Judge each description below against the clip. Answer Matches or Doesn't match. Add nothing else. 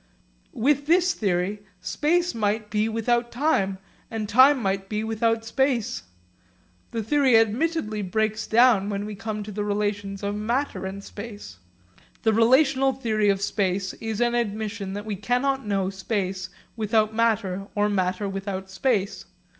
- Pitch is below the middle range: Doesn't match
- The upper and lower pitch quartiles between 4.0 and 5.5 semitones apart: Doesn't match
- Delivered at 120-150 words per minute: Matches